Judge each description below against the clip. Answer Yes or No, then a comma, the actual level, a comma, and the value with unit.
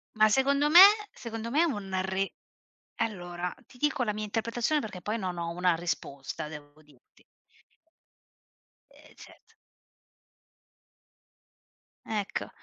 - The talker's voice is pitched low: No, high, 205 Hz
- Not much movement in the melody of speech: No, average, 5.0 semitones